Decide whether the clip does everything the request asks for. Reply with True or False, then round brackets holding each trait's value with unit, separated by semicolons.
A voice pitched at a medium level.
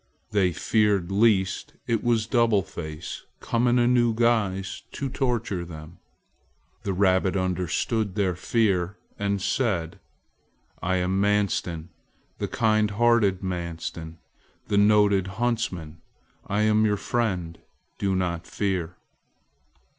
False (100 Hz)